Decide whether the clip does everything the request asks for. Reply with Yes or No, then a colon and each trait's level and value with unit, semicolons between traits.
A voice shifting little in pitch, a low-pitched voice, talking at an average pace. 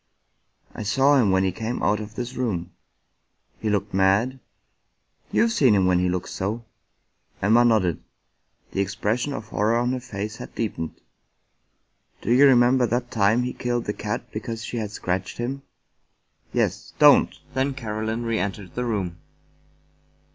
No: average, 3.6 semitones; low, 110 Hz; average, 160 wpm